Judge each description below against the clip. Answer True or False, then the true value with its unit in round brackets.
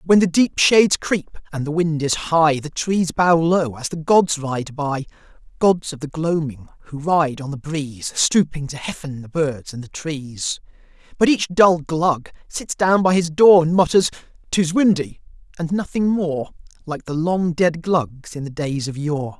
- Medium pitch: True (160 Hz)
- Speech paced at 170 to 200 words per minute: True (190 wpm)